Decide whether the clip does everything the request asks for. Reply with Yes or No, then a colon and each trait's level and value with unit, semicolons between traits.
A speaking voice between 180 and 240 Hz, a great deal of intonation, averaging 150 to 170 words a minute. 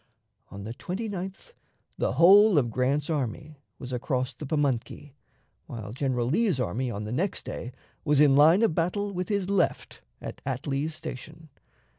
No: medium, 145 Hz; wide, 6.0 semitones; average, 155 wpm